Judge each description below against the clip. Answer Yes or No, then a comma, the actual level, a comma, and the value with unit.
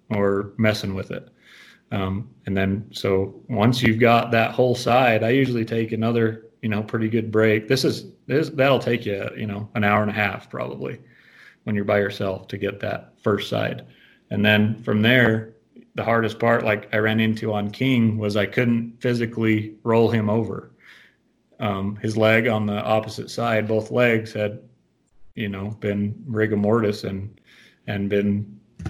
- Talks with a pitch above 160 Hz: No, low, 110 Hz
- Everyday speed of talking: Yes, average, 175 wpm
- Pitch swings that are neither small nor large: No, narrow, 1.8 semitones